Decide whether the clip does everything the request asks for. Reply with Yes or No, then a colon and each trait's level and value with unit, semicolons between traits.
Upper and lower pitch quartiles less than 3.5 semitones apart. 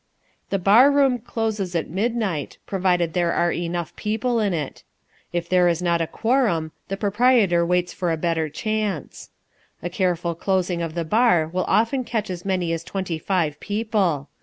No: average, 4.1 semitones